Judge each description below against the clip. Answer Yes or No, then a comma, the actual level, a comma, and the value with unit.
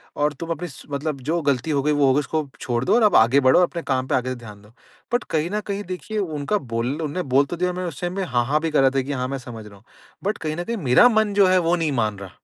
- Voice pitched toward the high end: No, medium, 150 Hz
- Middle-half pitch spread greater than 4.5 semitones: Yes, wide, 5.5 semitones